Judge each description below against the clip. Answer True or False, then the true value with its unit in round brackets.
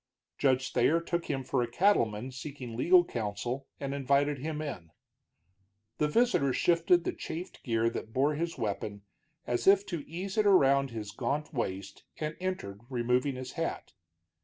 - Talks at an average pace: True (160 wpm)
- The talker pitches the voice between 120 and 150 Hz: True (140 Hz)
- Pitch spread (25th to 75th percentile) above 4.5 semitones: True (5.6 semitones)